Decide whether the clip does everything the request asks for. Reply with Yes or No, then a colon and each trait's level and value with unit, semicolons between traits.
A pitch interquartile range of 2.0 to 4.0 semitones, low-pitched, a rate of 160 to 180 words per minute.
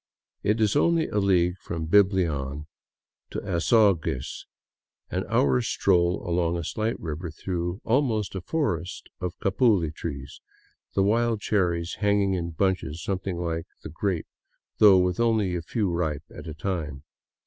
No: average, 3.7 semitones; very low, 90 Hz; average, 145 wpm